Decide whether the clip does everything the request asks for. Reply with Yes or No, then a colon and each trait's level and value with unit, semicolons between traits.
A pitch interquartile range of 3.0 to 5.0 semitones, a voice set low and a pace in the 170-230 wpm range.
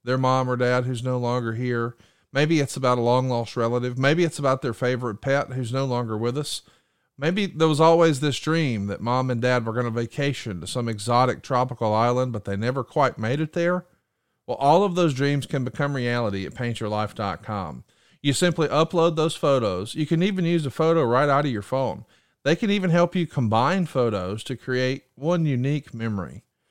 Yes: average, 4.1 semitones; low, 130 Hz; average, 200 wpm